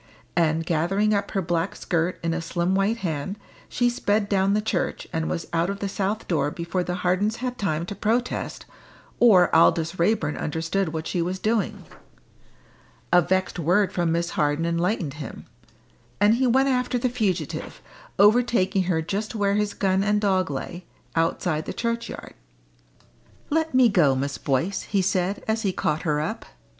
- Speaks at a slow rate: No, average, 170 wpm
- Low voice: No, medium, 185 Hz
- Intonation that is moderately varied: Yes, average, 3.9 semitones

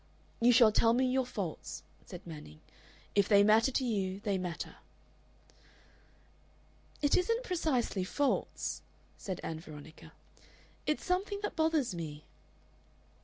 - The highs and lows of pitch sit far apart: Yes, wide, 8.1 semitones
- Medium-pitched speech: No, high, 215 Hz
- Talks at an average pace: No, slow, 120 wpm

